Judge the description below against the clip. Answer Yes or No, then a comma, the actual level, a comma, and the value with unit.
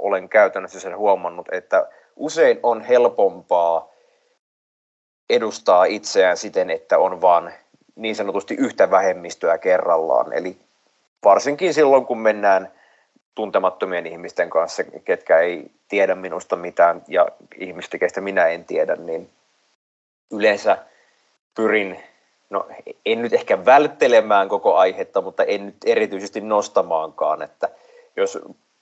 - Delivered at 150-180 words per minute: No, average, 115 wpm